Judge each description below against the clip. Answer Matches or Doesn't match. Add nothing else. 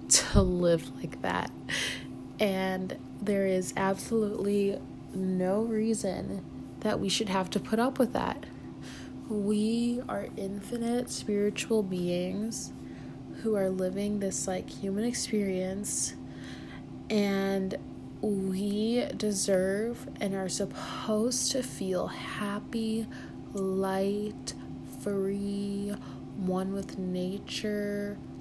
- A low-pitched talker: Doesn't match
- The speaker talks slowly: Matches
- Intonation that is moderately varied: Doesn't match